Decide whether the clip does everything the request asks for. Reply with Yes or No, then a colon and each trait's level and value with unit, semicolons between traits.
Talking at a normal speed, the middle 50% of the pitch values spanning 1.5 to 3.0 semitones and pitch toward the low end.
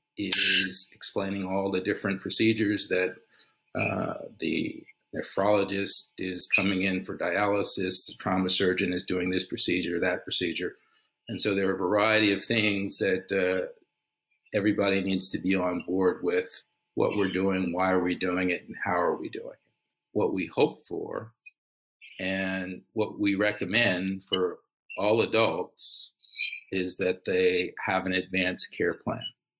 Yes: average, 150 wpm; narrow, 2.4 semitones; very low, 95 Hz